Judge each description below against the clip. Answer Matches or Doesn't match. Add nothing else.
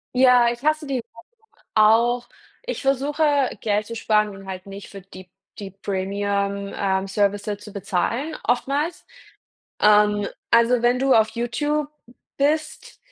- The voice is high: Matches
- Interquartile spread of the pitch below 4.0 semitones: Doesn't match